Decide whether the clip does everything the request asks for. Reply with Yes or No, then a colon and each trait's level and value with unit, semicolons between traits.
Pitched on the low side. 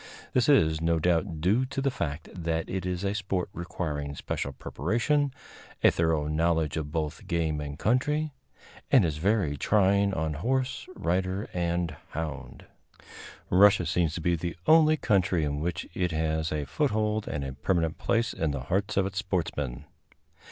Yes: very low, 85 Hz